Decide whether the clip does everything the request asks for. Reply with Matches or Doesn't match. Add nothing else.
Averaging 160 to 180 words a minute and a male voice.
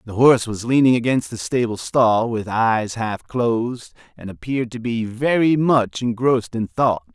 Matches